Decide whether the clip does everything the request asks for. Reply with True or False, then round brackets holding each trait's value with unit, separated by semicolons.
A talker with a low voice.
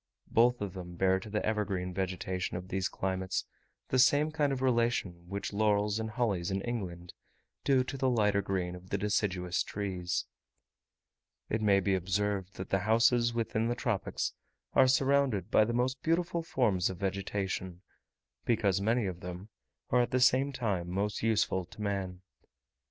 True (100 Hz)